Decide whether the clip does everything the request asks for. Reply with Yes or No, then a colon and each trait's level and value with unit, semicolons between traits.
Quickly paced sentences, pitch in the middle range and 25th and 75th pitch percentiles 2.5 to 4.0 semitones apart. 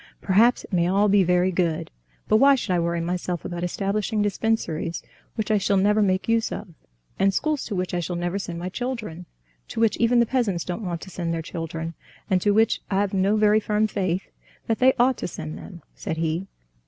No: fast, 215 wpm; high, 195 Hz; average, 3.7 semitones